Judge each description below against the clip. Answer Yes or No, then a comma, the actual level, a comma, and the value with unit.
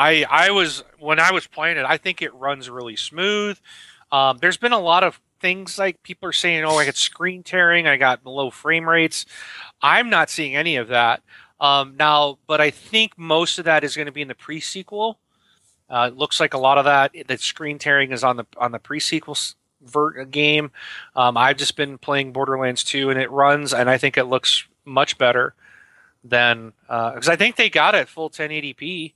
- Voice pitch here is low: No, medium, 150 Hz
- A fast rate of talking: Yes, fast, 210 wpm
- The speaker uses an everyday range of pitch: Yes, average, 3.9 semitones